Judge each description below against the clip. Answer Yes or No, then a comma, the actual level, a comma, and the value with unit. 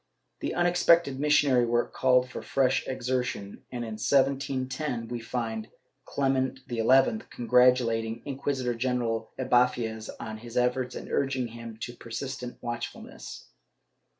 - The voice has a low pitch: Yes, low, 125 Hz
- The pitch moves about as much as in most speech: No, narrow, 2.2 semitones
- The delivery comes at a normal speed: No, slow, 125 wpm